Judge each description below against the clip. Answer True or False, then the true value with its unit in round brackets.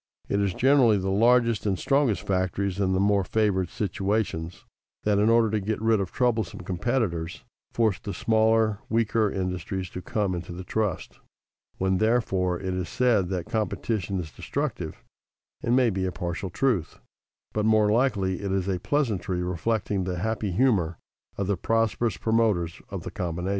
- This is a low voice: True (100 Hz)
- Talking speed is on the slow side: False (165 wpm)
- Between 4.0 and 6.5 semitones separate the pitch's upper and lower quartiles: False (3.4 semitones)